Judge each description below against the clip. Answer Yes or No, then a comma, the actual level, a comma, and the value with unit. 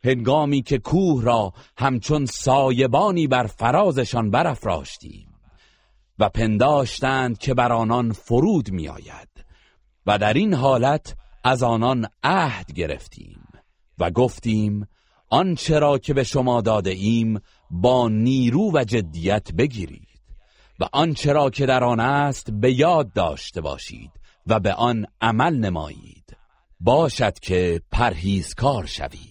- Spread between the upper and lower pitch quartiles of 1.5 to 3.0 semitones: No, average, 4.2 semitones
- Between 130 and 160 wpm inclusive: No, average, 120 wpm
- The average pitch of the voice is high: No, low, 125 Hz